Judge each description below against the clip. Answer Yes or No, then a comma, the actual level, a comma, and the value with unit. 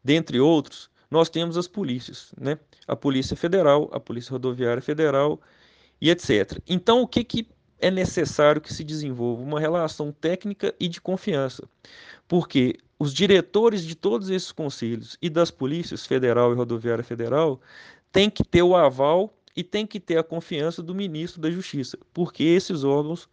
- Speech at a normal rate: Yes, average, 160 wpm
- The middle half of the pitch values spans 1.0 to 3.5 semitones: No, average, 4.4 semitones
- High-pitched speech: No, medium, 160 Hz